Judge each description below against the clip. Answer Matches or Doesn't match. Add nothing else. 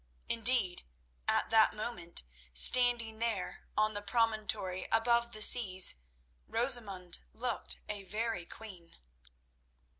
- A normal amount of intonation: Matches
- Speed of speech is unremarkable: Doesn't match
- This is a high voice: Matches